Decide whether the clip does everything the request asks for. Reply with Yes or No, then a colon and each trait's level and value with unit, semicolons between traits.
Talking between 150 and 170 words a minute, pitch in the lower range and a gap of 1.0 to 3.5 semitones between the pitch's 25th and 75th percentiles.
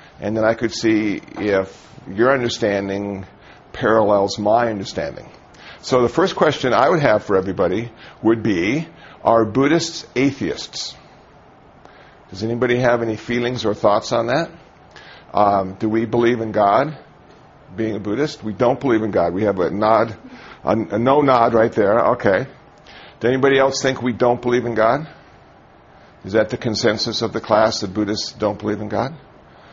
Yes: average, 165 wpm; low, 115 Hz; average, 2.7 semitones